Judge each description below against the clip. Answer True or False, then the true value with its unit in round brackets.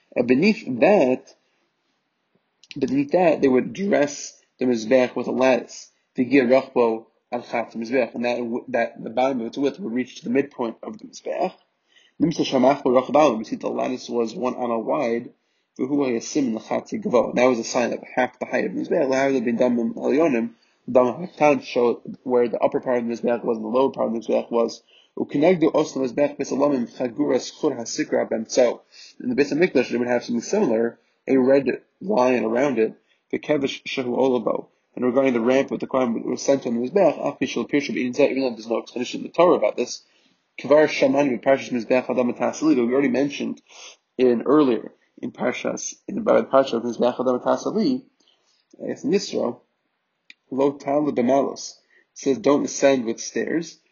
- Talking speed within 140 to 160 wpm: False (180 wpm)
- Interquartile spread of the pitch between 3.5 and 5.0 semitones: False (2.6 semitones)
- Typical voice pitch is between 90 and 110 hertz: False (130 Hz)